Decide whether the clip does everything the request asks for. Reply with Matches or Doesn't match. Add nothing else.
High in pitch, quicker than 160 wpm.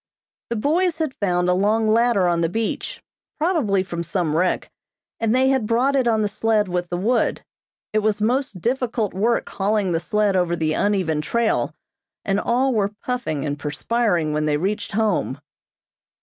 Matches